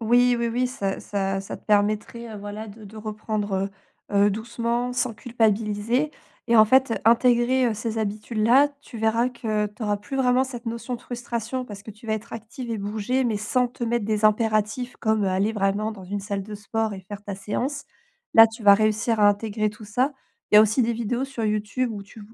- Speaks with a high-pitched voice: Yes, high, 220 Hz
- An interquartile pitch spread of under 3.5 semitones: Yes, narrow, 2.4 semitones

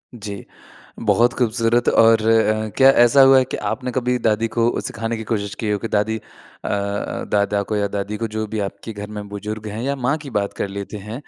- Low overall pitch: Yes, low, 110 Hz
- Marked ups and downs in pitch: No, narrow, 2.4 semitones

